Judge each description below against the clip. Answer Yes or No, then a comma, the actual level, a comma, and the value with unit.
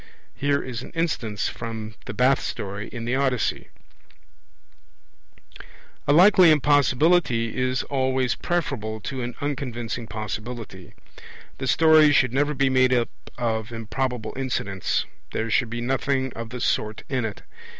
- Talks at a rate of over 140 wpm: No, slow, 135 wpm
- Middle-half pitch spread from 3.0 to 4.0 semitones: Yes, average, 3.4 semitones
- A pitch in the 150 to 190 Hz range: No, low, 125 Hz